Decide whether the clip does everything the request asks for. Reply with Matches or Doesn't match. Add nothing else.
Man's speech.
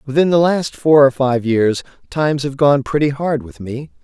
Matches